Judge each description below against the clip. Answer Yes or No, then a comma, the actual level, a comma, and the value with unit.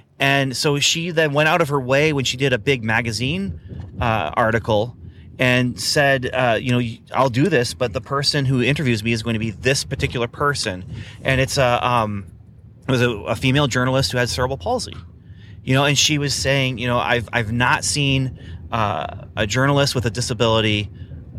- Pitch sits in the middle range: No, low, 125 Hz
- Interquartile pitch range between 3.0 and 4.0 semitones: Yes, average, 3.6 semitones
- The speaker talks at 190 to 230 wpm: Yes, average, 195 wpm